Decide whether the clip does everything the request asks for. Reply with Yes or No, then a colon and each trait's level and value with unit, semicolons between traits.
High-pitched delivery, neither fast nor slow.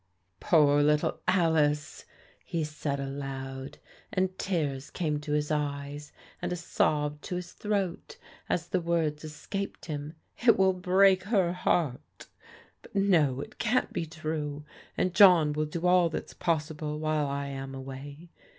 No: medium, 155 Hz; average, 155 wpm